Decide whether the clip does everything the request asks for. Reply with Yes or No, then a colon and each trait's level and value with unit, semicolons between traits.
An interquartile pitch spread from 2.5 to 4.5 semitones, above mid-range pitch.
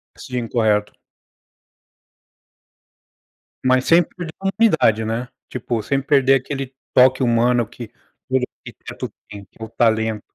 No: average, 3.2 semitones; low, 125 Hz